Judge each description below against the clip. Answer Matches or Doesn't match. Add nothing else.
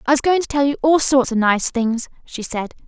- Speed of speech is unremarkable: Doesn't match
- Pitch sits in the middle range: Doesn't match